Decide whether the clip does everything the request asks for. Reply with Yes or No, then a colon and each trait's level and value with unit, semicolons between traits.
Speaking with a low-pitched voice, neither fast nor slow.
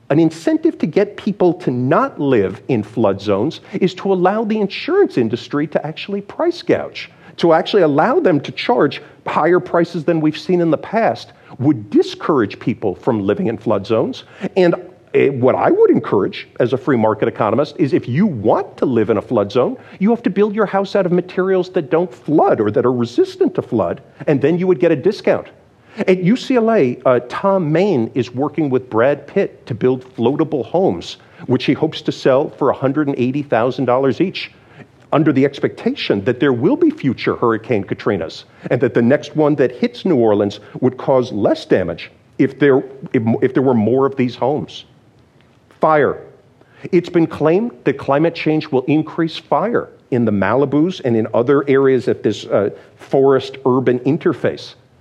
No: medium, 160 Hz; average, 180 wpm